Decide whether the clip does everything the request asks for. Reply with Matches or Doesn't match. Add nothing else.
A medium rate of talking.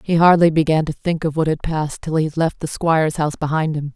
Doesn't match